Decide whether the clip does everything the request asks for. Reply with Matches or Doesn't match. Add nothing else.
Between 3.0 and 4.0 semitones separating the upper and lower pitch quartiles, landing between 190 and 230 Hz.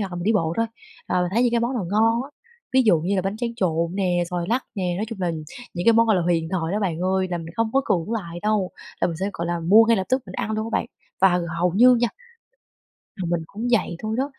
Doesn't match